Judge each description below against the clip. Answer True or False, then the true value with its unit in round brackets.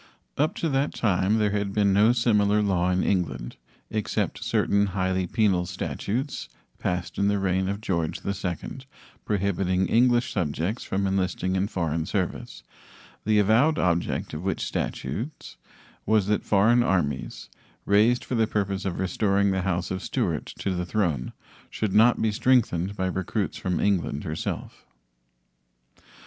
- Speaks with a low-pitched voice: True (100 Hz)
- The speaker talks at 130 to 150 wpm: True (145 wpm)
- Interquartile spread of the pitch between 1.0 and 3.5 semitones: True (2.8 semitones)